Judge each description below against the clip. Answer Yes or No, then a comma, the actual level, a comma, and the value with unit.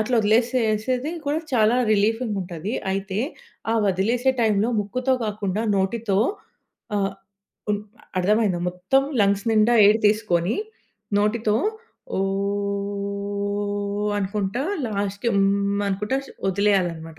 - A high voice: Yes, high, 205 Hz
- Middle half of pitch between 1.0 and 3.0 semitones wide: Yes, narrow, 2.4 semitones